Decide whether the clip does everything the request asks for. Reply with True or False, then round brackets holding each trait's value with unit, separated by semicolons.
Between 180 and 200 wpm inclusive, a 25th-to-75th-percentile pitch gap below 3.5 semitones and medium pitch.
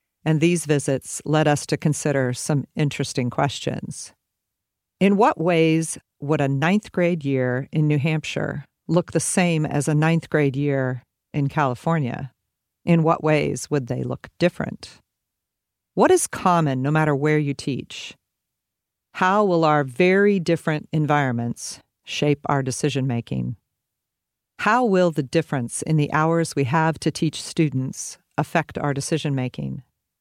False (145 wpm; 3.0 semitones; 150 Hz)